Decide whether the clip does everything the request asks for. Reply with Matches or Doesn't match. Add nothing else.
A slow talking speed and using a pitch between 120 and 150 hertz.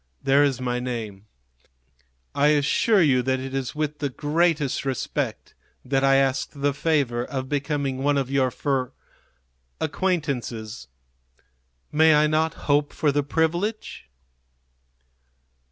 Matches